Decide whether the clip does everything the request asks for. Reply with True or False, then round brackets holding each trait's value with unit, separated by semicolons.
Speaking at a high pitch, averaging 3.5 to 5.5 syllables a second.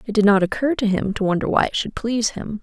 False (215 Hz; 6.4 syllables/s)